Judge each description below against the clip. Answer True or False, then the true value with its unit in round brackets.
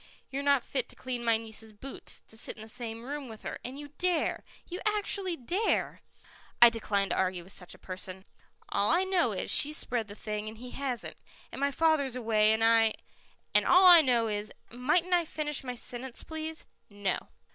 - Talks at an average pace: False (210 wpm)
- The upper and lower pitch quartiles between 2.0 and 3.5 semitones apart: False (5.5 semitones)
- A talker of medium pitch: False (245 Hz)